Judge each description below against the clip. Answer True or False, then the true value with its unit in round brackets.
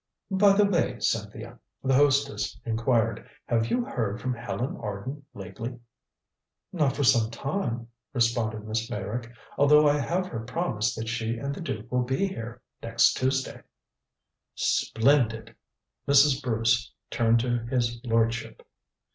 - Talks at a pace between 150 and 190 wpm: False (135 wpm)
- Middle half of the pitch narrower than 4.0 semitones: True (3.4 semitones)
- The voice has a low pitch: True (120 Hz)